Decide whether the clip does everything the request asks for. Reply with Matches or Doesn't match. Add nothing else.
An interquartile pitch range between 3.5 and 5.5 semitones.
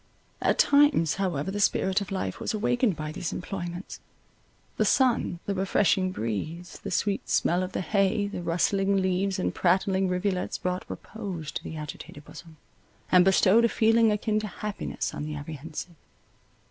Doesn't match